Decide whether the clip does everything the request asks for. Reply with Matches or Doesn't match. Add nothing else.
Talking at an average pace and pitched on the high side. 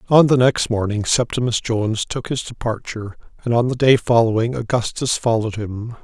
Doesn't match